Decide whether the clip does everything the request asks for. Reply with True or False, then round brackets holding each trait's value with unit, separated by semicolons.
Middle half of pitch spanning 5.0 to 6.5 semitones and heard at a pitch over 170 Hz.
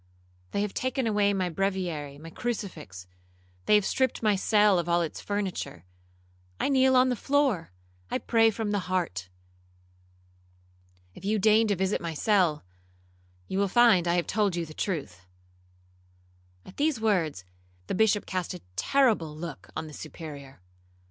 True (5.6 semitones; 185 Hz)